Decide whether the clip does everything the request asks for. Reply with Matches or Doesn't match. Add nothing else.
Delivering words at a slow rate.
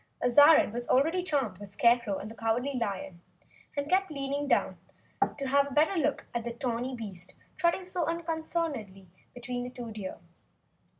Doesn't match